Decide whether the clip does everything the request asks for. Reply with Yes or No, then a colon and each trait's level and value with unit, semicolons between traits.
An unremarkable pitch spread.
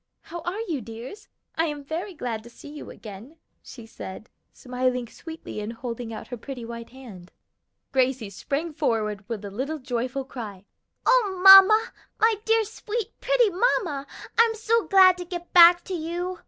No: wide, 8.1 semitones